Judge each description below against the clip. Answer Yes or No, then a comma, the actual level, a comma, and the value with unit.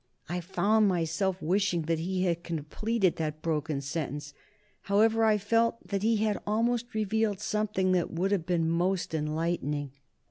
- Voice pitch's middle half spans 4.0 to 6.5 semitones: Yes, average, 4.5 semitones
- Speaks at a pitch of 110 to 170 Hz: No, medium, 185 Hz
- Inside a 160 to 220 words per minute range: No, average, 150 wpm